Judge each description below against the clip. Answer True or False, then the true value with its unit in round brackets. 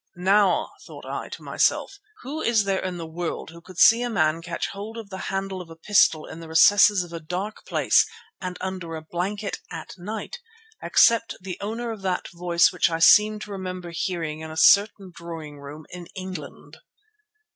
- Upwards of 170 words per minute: True (190 wpm)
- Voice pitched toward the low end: False (185 Hz)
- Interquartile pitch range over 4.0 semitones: False (3.5 semitones)